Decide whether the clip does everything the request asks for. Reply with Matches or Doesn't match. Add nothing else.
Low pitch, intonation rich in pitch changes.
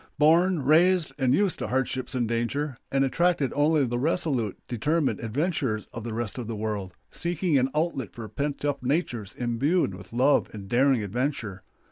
Doesn't match